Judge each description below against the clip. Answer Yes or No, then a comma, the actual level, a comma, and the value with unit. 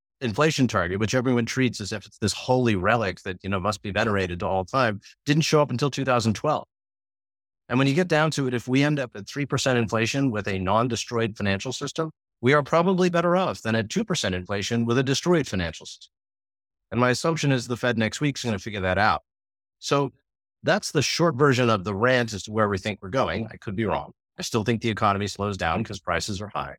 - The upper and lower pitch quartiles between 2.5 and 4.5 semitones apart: No, average, 5.3 semitones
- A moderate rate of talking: No, fast, 235 wpm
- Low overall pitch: Yes, low, 115 Hz